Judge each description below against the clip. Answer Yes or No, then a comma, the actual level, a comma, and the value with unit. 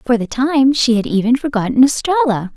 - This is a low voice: No, very high, 255 Hz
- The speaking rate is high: No, average, 190 wpm